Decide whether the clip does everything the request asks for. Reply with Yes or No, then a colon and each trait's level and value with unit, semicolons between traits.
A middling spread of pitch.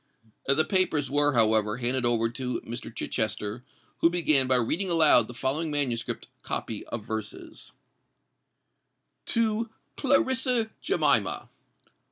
No: wide, 6.4 semitones